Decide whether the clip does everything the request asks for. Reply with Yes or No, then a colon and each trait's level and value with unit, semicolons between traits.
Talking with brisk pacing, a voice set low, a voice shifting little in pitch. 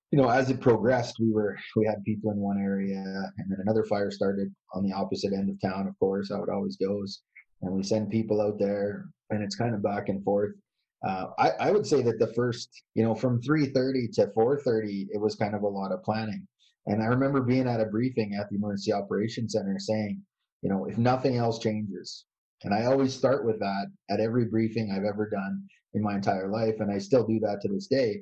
Yes: fast, 230 wpm; low, 105 Hz; narrow, 2.2 semitones